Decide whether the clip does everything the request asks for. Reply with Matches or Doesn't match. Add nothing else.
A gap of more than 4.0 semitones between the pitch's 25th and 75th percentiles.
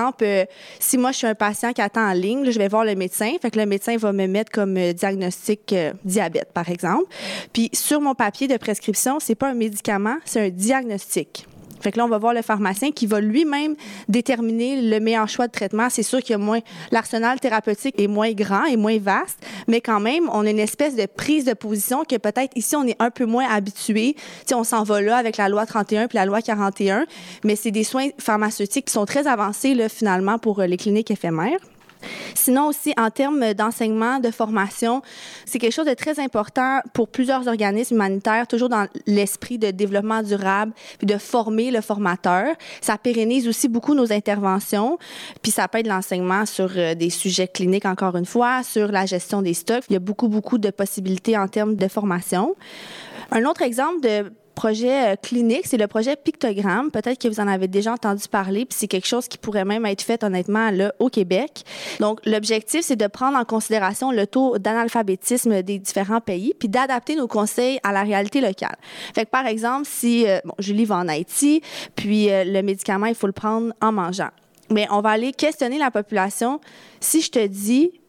Doesn't match